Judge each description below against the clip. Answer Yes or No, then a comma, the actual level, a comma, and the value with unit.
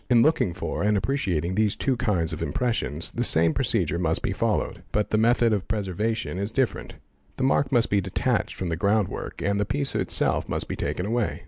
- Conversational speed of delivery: No, fast, 210 wpm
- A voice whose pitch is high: No, low, 105 Hz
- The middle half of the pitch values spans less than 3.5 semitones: No, average, 4.4 semitones